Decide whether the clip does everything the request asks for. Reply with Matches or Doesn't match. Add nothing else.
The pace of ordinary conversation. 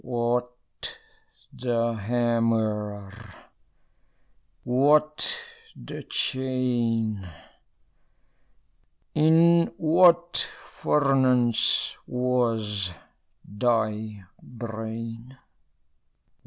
Doesn't match